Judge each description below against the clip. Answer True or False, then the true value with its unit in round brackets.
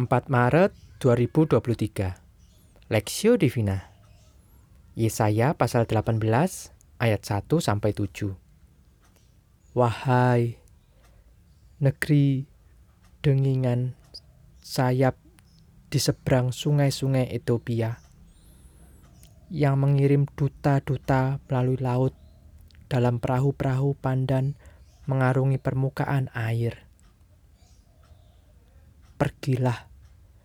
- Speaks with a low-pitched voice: True (120 Hz)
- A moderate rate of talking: False (65 wpm)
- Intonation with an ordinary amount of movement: False (6.0 semitones)